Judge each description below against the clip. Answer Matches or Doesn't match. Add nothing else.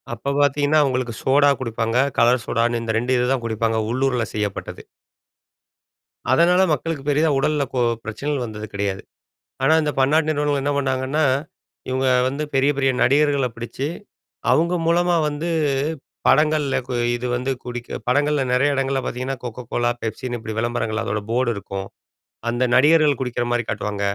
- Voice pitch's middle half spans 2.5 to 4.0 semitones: Matches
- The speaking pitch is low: Matches